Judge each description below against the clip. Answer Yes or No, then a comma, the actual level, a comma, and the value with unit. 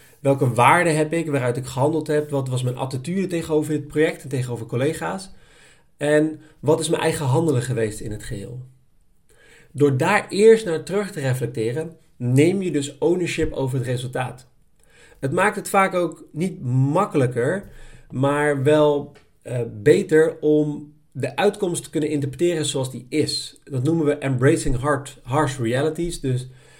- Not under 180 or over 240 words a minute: No, average, 155 wpm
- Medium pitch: Yes, medium, 150 Hz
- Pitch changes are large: No, average, 3.3 semitones